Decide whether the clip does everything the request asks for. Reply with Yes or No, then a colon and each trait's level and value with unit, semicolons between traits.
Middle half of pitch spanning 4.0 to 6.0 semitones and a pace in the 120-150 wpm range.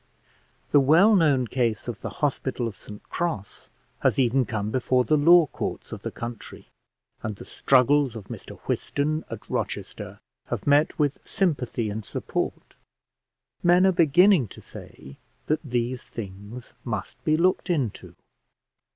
Yes: average, 5.2 semitones; average, 145 wpm